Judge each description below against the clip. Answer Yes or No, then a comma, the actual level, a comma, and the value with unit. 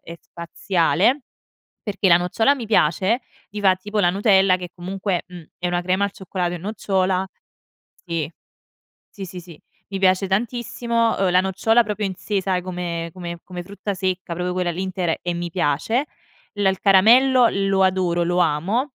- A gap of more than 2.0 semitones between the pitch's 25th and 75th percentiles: Yes, narrow, 2.5 semitones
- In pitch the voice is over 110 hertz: Yes, medium, 185 Hz